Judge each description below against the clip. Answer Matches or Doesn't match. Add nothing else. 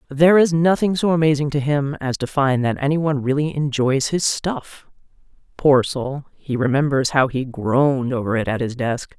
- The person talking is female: Matches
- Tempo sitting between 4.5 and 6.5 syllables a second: Matches